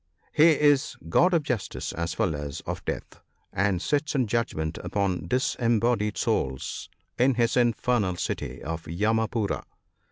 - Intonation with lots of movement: Yes, wide, 6.3 semitones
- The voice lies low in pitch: Yes, low, 110 Hz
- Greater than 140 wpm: No, slow, 135 wpm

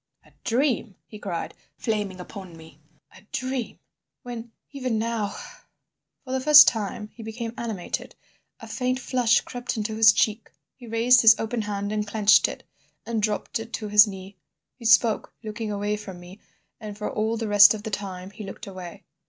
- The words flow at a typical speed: Yes, average, 175 wpm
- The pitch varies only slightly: Yes, narrow, 2.3 semitones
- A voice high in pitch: Yes, high, 215 Hz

